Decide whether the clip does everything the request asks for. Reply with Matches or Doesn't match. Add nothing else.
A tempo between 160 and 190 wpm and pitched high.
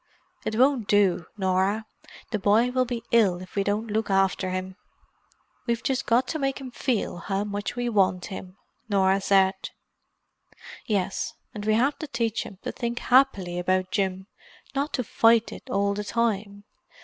Matches